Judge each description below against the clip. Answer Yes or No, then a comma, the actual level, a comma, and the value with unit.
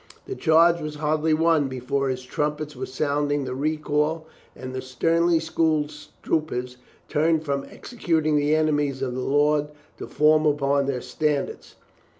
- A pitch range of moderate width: No, narrow, 2.2 semitones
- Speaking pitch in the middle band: Yes, medium, 150 Hz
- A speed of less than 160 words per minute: Yes, average, 150 wpm